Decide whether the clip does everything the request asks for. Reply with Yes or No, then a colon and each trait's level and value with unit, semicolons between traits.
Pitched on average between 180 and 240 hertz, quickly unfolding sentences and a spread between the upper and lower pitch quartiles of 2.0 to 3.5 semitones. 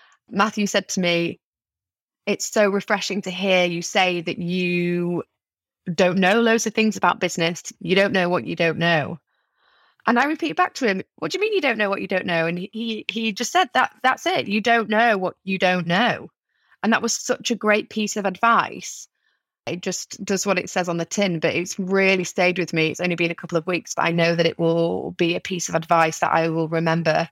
No: medium, 185 Hz; fast, 235 wpm; average, 4.3 semitones